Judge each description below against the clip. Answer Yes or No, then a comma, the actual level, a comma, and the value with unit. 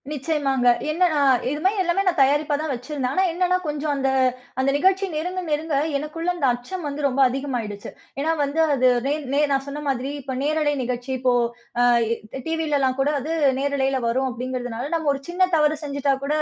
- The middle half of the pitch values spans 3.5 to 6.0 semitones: No, average, 3.0 semitones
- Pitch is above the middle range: Yes, very high, 285 Hz